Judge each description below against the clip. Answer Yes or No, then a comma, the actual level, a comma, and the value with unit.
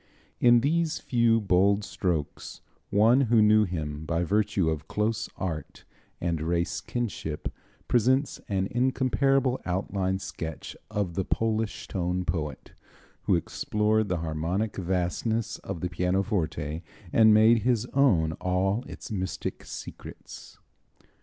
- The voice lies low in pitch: Yes, low, 100 Hz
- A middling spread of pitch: Yes, average, 4.5 semitones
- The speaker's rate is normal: No, slow, 120 wpm